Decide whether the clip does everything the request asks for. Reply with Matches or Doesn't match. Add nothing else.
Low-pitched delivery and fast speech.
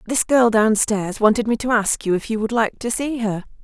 Doesn't match